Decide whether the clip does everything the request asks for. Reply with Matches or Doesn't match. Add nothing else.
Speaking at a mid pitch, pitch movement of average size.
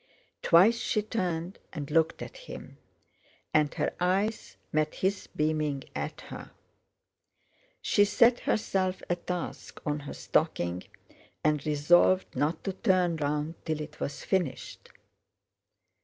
Matches